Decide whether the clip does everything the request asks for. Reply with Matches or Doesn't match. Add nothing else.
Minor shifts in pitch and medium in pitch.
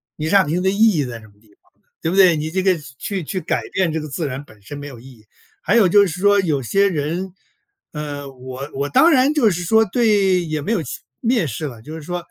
Doesn't match